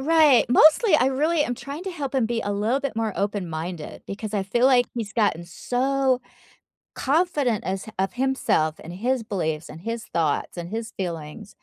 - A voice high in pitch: Yes, high, 230 Hz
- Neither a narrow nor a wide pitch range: No, wide, 5.7 semitones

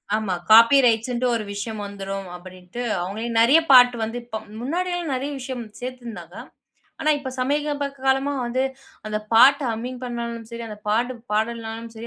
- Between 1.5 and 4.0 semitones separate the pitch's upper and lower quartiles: Yes, average, 2.9 semitones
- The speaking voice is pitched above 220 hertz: Yes, high, 235 Hz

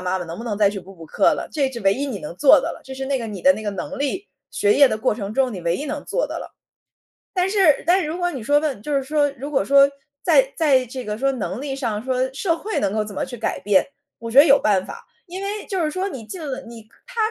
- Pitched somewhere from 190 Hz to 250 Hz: No, very high, 265 Hz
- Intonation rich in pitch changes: Yes, wide, 6.0 semitones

